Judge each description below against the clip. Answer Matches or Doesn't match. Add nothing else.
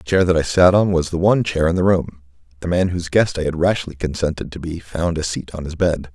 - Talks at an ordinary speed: Doesn't match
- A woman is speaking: Doesn't match